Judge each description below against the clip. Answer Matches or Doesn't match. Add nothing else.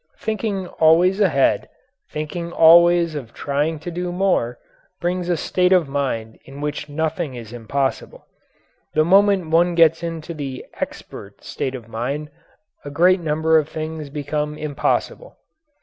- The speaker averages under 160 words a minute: Matches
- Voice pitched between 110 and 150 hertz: Doesn't match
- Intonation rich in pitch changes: Doesn't match